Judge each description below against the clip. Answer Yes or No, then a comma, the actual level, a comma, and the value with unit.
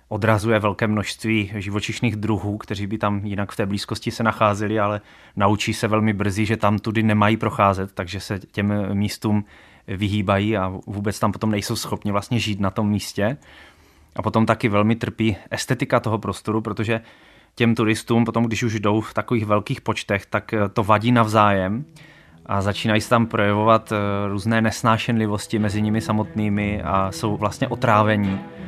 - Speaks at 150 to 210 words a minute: Yes, average, 160 wpm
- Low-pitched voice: Yes, low, 105 Hz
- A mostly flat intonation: Yes, narrow, 1.6 semitones